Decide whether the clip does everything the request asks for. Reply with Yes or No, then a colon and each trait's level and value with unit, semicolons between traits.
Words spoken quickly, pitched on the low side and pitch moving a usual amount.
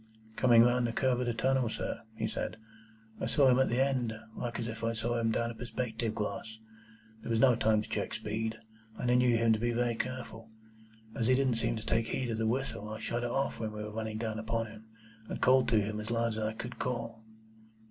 No: fast, 240 wpm; low, 115 Hz; narrow, 1.8 semitones